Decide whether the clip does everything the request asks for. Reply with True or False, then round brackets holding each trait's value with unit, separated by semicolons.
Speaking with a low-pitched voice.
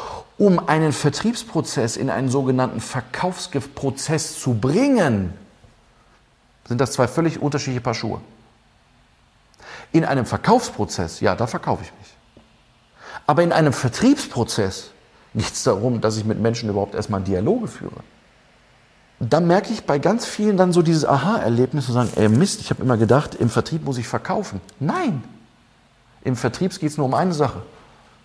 True (130 Hz)